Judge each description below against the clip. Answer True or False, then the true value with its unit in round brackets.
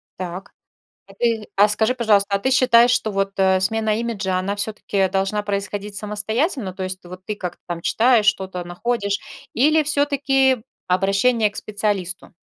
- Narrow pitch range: False (3.5 semitones)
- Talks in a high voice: True (205 Hz)